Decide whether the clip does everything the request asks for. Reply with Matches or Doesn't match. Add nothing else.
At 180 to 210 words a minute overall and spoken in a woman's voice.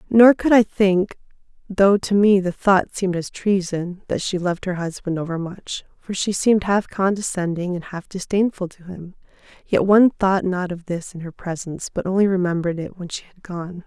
Matches